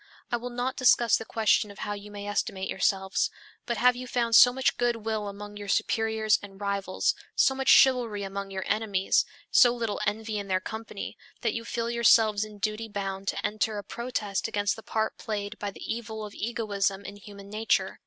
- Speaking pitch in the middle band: No, high, 215 Hz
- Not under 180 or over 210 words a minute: Yes, average, 200 wpm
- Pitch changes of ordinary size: No, narrow, 2.3 semitones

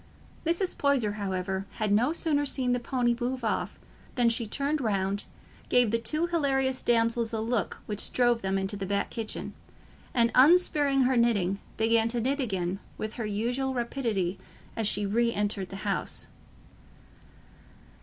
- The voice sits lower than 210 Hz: No, high, 230 Hz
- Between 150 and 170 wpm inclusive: Yes, average, 155 wpm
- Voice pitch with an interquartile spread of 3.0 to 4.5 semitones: Yes, average, 4.2 semitones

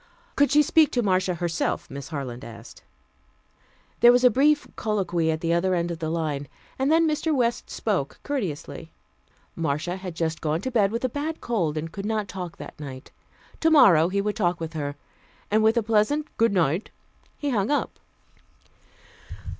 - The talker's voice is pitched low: No, high, 190 Hz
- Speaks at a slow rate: No, average, 175 wpm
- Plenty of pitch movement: Yes, wide, 7.0 semitones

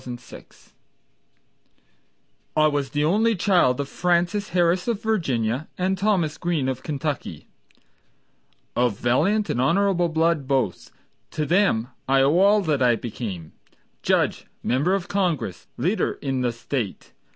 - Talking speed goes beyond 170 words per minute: No, slow, 135 wpm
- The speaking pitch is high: No, medium, 155 Hz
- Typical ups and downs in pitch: No, wide, 6.4 semitones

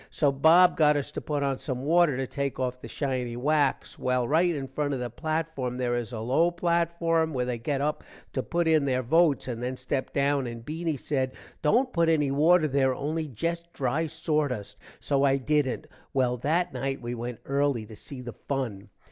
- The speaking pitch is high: No, medium, 140 Hz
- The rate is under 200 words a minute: No, fast, 205 wpm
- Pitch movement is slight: No, average, 3.9 semitones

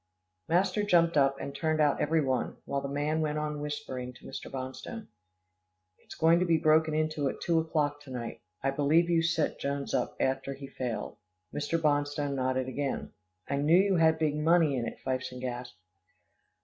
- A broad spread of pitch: No, average, 2.9 semitones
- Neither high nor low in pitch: Yes, medium, 145 Hz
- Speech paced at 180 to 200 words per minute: Yes, average, 185 wpm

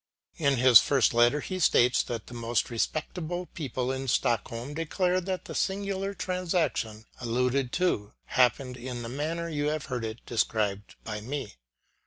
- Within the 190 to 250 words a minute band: No, average, 150 wpm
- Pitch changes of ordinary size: No, wide, 5.9 semitones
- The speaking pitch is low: Yes, low, 130 Hz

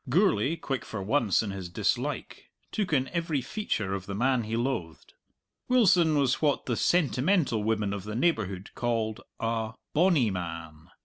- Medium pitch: No, low, 115 Hz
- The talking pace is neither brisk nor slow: Yes, average, 160 wpm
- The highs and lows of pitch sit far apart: Yes, wide, 6.9 semitones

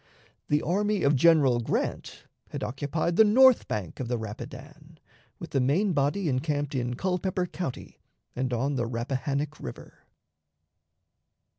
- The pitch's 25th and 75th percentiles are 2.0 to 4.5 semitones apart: No, average, 5.1 semitones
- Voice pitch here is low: No, medium, 145 Hz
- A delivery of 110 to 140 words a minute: Yes, slow, 135 wpm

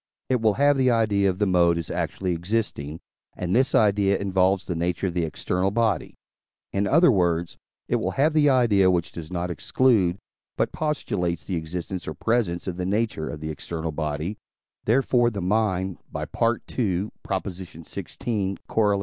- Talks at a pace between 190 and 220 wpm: No, average, 165 wpm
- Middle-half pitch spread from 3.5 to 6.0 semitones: Yes, average, 4.4 semitones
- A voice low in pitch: Yes, very low, 95 Hz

